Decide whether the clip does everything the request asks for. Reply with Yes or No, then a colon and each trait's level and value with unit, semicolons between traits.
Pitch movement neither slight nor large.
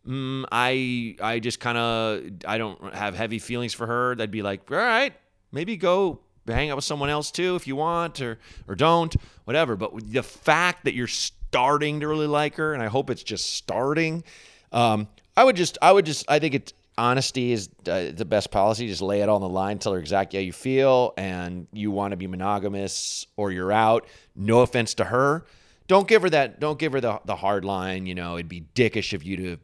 No: wide, 6.5 semitones